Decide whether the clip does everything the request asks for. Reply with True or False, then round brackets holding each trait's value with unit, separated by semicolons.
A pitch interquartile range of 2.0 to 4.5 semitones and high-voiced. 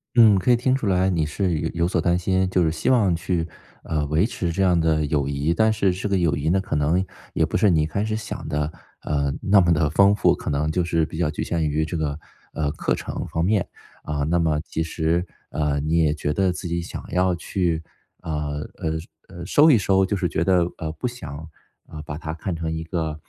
False (3.3 semitones; 85 Hz)